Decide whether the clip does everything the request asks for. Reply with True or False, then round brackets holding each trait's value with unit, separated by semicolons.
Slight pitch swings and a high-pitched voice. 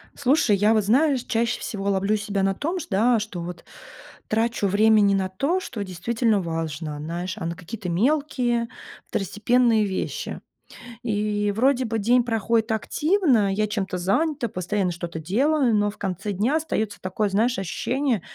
False (3.9 semitones; 215 Hz)